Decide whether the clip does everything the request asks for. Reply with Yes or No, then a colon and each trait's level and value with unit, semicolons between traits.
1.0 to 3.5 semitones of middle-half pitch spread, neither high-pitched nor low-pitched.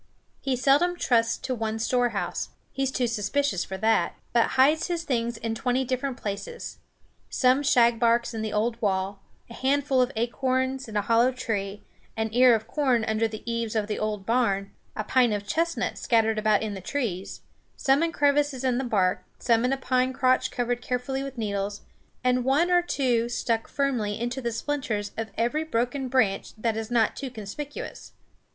No: average, 3.2 semitones; high, 240 Hz